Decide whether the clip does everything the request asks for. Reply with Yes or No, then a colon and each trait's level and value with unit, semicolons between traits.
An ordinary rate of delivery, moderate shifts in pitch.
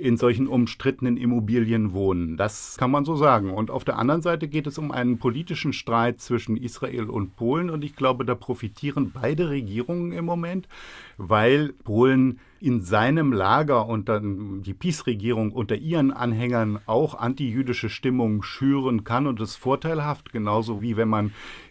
Yes: average, 160 wpm; average, 3.8 semitones